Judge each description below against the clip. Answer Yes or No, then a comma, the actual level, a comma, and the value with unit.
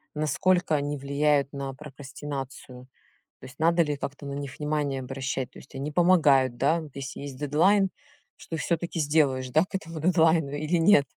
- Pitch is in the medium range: Yes, medium, 145 Hz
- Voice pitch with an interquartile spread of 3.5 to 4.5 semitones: No, average, 2.9 semitones